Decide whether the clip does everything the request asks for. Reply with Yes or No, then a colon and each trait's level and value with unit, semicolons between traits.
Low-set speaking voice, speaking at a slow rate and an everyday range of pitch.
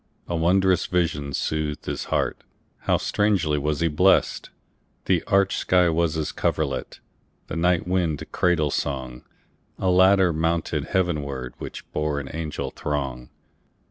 Yes: very low, 80 Hz; slow, 110 wpm; average, 3.5 semitones